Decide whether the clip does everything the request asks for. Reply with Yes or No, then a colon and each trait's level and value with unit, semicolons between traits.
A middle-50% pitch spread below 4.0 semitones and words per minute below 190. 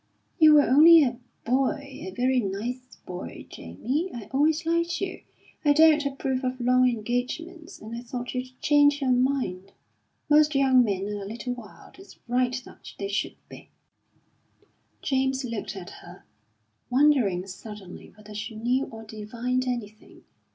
No: average, 4.5 semitones; average, 150 wpm